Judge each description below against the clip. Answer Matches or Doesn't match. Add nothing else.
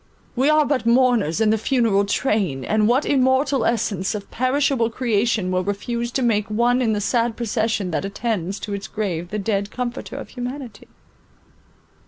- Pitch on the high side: Matches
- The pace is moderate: Matches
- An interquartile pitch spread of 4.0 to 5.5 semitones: Doesn't match